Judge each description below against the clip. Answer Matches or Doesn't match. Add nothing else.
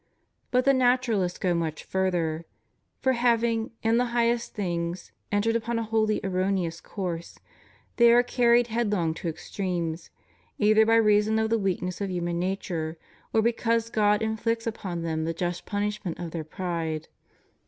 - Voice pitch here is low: Doesn't match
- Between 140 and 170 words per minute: Matches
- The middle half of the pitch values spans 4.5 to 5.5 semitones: Matches